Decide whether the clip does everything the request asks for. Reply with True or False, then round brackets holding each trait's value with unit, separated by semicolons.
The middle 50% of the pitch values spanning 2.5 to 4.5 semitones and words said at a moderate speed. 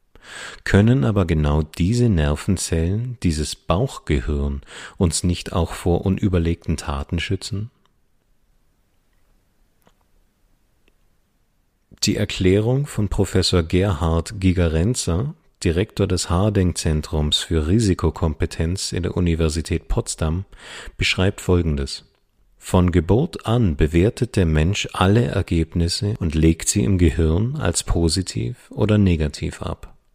False (3.7 semitones; 100 wpm)